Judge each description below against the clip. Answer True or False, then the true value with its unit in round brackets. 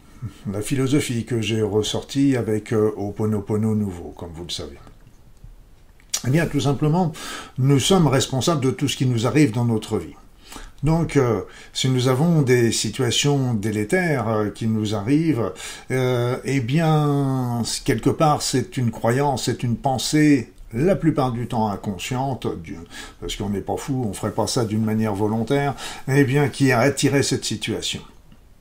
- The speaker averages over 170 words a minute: False (155 wpm)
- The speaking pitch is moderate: False (125 Hz)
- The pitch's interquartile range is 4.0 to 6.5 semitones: True (4.5 semitones)